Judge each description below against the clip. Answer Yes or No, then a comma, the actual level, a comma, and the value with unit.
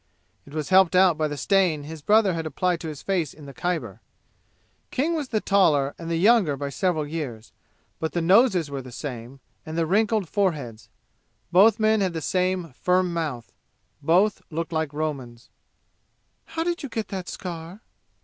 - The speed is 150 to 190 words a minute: Yes, average, 180 wpm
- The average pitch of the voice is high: No, medium, 170 Hz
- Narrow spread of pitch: No, average, 4.5 semitones